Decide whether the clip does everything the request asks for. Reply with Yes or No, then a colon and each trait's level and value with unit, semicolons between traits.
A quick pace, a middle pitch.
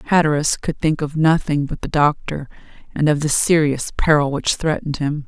No: average, 180 wpm; medium, 150 Hz